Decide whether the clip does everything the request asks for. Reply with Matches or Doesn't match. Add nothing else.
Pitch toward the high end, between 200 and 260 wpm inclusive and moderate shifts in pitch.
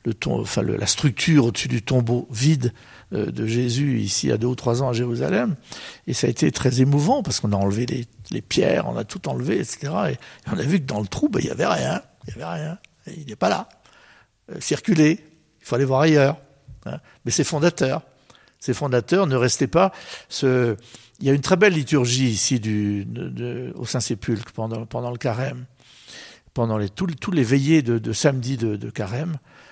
Doesn't match